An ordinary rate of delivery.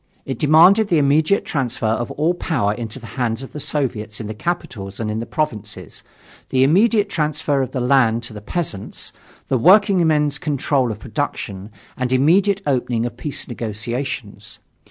Yes: average, 165 wpm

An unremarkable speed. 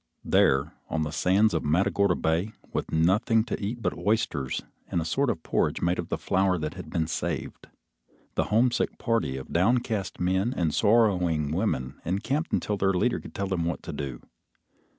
Yes: average, 180 wpm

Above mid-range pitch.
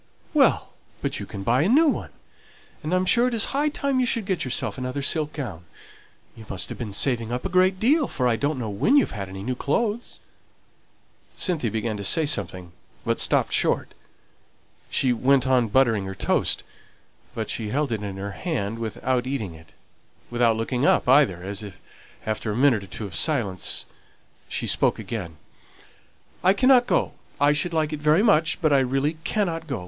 No: low, 130 Hz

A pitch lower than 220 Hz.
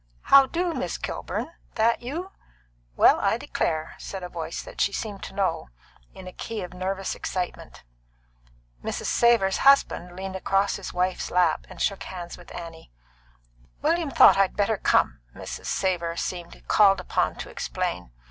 Yes: high, 190 Hz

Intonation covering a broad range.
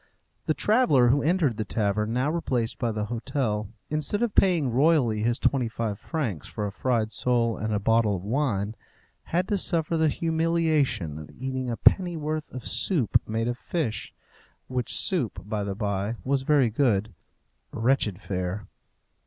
Yes: wide, 6.1 semitones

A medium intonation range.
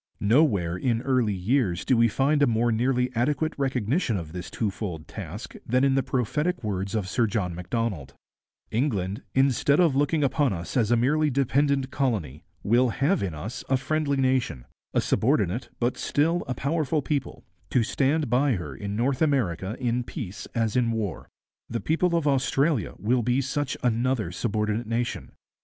Yes: average, 4.7 semitones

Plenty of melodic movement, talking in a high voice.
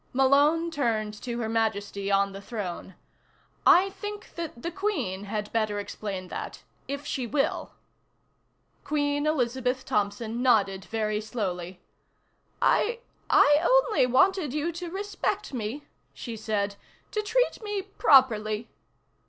Yes: wide, 7.8 semitones; high, 245 Hz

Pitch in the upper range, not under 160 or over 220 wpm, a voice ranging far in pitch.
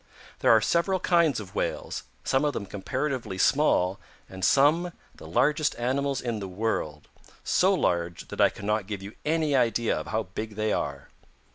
No: low, 115 Hz; average, 170 wpm; wide, 6.9 semitones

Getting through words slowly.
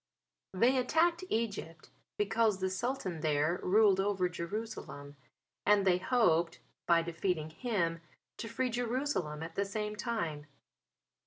Yes: slow, 125 wpm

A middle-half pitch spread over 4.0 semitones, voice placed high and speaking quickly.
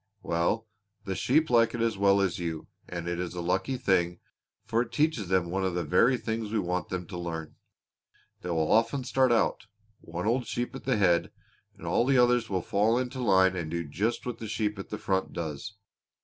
No: average, 5.0 semitones; low, 100 Hz; fast, 215 wpm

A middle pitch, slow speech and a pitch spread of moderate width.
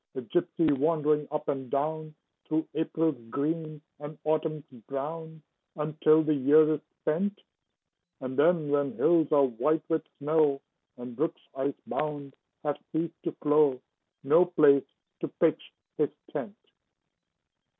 No: medium, 150 Hz; slow, 130 wpm; narrow, 1.9 semitones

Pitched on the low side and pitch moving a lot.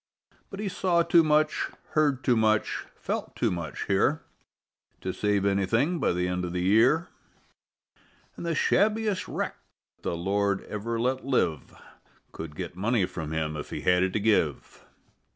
Yes: low, 105 Hz; wide, 8.9 semitones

